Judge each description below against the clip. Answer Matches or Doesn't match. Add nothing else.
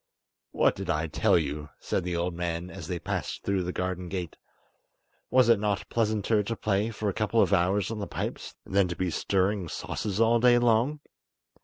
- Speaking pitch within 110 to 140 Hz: Doesn't match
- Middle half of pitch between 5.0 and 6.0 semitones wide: Doesn't match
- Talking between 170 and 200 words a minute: Matches